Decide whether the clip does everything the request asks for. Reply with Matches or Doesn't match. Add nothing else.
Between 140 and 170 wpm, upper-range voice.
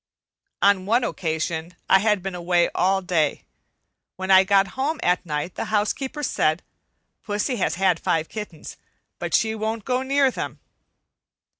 Matches